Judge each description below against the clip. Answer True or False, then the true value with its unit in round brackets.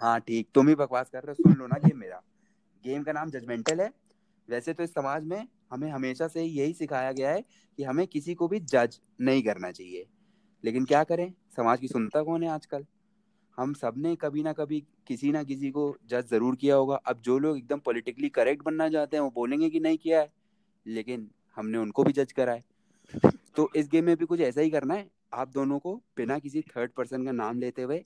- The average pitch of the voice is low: False (150 Hz)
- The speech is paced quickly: True (225 wpm)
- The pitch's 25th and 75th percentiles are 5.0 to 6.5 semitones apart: True (5.5 semitones)